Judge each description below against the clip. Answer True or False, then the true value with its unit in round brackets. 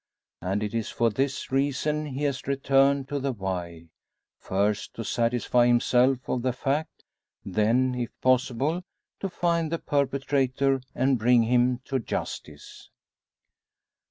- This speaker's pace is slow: True (130 wpm)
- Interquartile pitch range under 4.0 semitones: True (2.9 semitones)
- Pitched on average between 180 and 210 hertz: False (130 Hz)